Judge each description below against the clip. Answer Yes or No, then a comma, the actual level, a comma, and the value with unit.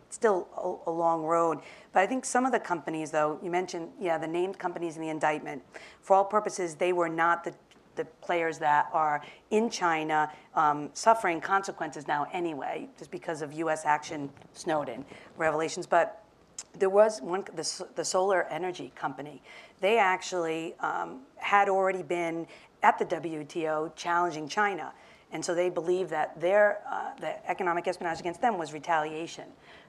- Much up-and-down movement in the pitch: No, average, 2.8 semitones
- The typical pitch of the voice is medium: Yes, medium, 170 Hz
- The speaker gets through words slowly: No, average, 160 wpm